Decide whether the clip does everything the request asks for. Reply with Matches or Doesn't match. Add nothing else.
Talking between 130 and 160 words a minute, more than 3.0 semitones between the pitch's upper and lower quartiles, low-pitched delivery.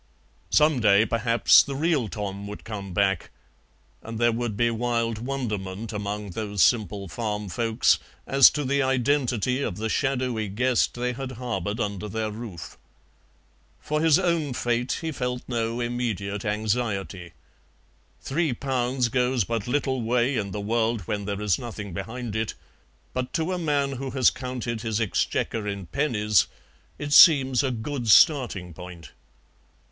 Matches